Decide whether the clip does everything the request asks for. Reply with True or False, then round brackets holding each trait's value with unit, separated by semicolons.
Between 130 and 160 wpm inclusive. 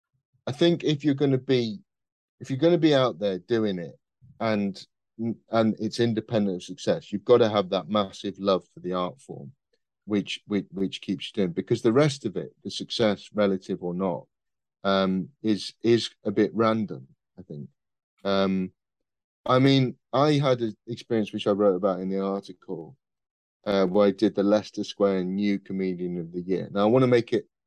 False (190 wpm)